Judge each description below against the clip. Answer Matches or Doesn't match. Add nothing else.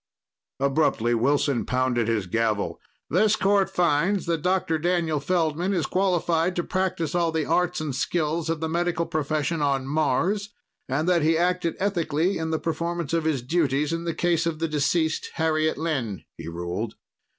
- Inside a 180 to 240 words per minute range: Doesn't match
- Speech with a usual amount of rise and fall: Matches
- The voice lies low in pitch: Doesn't match